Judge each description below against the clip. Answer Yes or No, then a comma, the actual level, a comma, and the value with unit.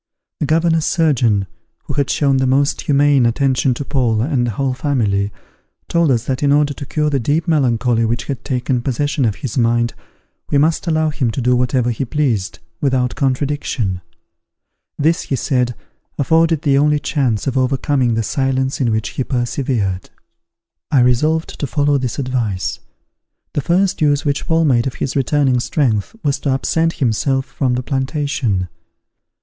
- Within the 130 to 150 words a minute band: No, average, 165 wpm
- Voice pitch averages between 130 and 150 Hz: Yes, low, 135 Hz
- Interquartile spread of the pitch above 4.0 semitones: No, average, 3.2 semitones